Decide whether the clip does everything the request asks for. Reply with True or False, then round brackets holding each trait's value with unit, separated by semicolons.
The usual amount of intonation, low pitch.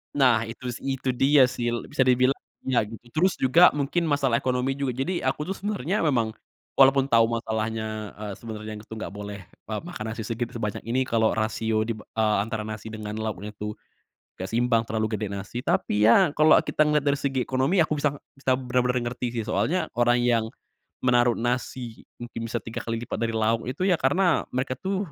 True (3.4 semitones; 120 Hz)